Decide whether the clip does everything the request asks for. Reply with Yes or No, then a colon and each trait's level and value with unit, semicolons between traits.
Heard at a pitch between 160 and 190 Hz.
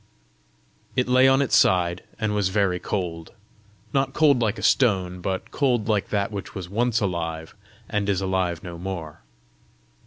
No: low, 100 Hz